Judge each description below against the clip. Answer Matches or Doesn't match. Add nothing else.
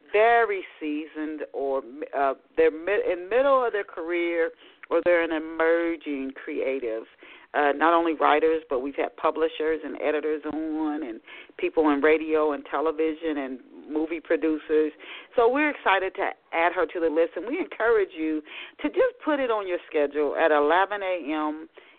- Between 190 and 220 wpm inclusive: Doesn't match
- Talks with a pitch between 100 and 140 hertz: Doesn't match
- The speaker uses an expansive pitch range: Matches